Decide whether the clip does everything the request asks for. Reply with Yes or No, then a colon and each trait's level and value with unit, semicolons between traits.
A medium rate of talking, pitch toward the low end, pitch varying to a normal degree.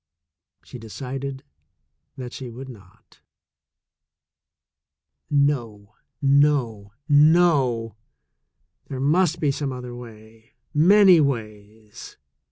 No: slow, 85 wpm; low, 130 Hz; average, 4.4 semitones